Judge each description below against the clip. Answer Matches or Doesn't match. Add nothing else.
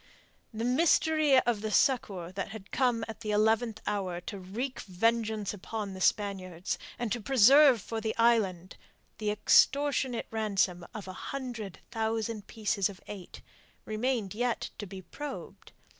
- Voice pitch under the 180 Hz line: Doesn't match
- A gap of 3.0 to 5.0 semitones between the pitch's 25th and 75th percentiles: Matches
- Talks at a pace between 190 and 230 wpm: Doesn't match